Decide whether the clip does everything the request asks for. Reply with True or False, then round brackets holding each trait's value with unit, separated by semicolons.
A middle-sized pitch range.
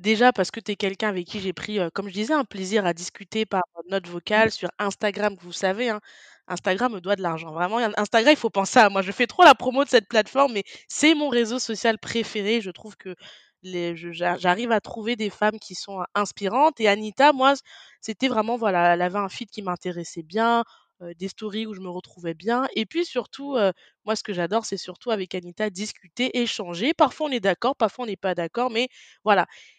True (4.2 semitones)